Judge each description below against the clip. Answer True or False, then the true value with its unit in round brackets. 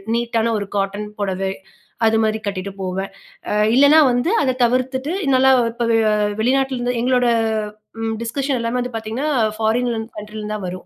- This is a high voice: True (230 Hz)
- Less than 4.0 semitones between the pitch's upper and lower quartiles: True (3.3 semitones)